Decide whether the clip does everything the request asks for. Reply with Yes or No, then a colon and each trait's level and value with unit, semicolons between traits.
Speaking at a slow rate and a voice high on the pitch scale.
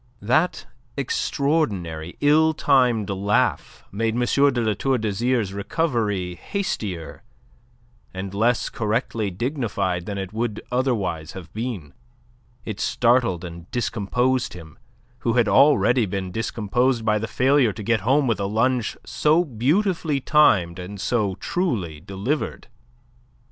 No: slow, 125 wpm; low, 115 Hz